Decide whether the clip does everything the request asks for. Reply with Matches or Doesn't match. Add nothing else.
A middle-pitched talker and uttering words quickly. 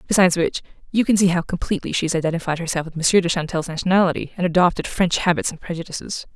Matches